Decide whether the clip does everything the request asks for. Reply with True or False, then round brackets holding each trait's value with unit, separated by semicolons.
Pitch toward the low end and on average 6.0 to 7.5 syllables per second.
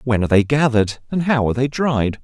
True (125 Hz; 6.4 syllables/s)